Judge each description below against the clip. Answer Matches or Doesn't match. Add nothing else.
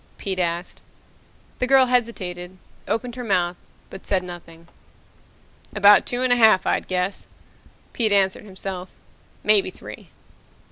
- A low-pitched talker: Doesn't match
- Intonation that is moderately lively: Matches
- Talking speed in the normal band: Doesn't match